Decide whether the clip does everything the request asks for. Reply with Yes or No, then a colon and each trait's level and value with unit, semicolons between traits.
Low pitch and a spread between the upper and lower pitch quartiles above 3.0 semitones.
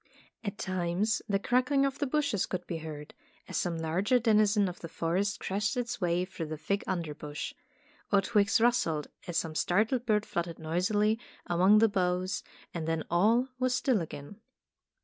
No: high, 195 Hz; average, 4.6 semitones